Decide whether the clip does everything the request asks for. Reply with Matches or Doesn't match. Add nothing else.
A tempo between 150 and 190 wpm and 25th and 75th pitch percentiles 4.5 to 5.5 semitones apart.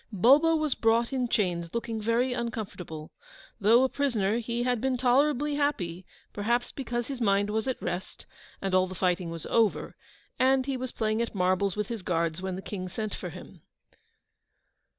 Matches